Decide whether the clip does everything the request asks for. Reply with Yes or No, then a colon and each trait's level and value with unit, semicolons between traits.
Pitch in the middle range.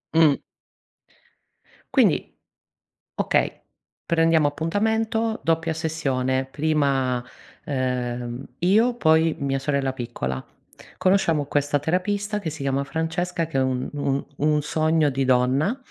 Yes: medium, 150 Hz